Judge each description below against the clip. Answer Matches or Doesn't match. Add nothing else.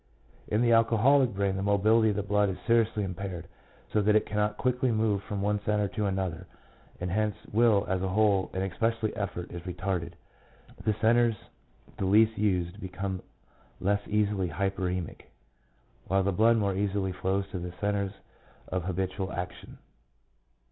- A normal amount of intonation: Doesn't match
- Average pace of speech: Matches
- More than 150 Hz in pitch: Doesn't match